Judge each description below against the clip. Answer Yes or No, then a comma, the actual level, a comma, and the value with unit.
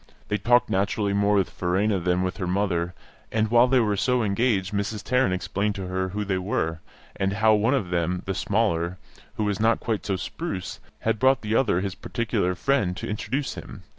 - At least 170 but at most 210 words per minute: Yes, average, 200 wpm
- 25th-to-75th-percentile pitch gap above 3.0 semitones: Yes, average, 3.4 semitones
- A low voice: Yes, low, 100 Hz